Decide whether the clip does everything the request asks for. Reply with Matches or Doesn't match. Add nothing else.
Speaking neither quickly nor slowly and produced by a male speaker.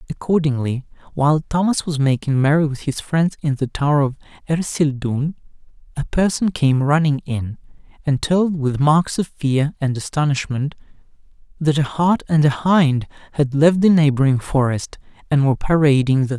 Matches